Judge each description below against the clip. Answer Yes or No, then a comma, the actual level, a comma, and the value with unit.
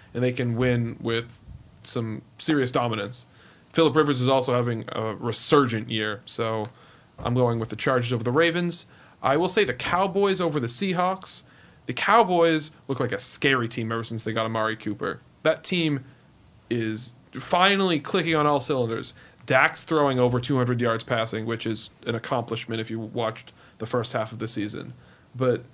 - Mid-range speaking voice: No, low, 120 Hz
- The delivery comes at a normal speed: Yes, average, 175 wpm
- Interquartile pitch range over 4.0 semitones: Yes, average, 4.7 semitones